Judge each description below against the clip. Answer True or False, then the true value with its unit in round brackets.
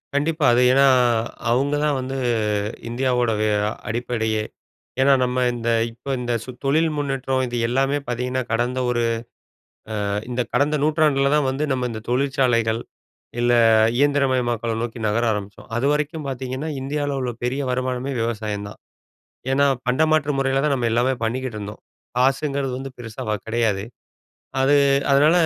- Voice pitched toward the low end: True (130 Hz)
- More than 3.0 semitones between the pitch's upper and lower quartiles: False (2.7 semitones)